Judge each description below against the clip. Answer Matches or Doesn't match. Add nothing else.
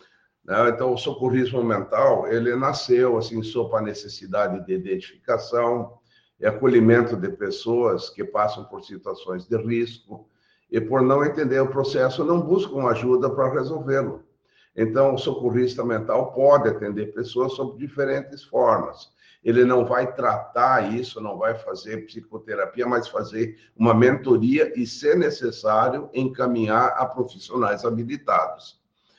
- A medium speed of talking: Matches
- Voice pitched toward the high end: Doesn't match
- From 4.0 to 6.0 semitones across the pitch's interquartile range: Doesn't match